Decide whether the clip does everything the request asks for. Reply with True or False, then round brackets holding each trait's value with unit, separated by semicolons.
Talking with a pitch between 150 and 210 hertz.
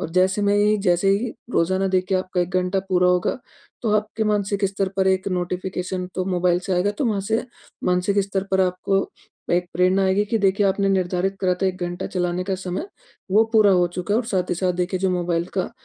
True (190 Hz)